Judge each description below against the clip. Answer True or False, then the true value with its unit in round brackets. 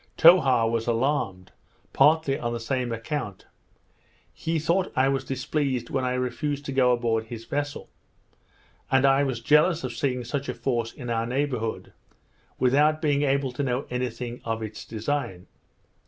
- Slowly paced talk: False (160 wpm)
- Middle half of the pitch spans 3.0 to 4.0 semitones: True (3.5 semitones)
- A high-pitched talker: False (130 Hz)